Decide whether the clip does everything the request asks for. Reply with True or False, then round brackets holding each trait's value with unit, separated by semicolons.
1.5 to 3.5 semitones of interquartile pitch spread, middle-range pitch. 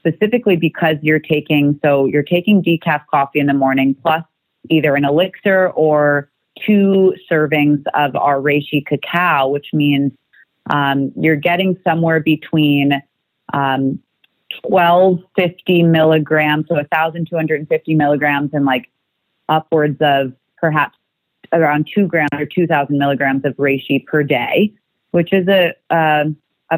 True (2.9 semitones; 155 Hz)